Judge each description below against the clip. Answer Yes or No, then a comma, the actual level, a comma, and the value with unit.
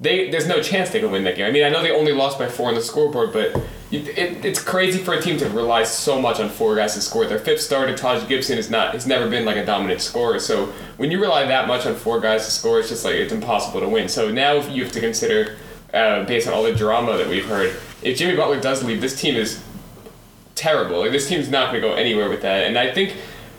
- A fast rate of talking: Yes, fast, 265 wpm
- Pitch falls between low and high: Yes, medium, 145 Hz